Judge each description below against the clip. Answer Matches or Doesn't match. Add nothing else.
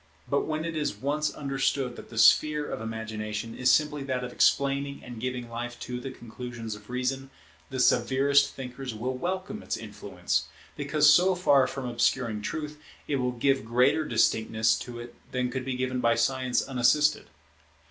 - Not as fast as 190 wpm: Matches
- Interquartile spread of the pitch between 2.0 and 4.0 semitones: Matches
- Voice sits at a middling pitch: Doesn't match